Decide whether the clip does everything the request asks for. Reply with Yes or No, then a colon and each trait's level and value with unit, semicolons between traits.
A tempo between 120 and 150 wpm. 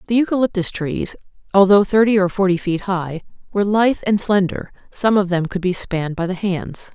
No: average, 190 wpm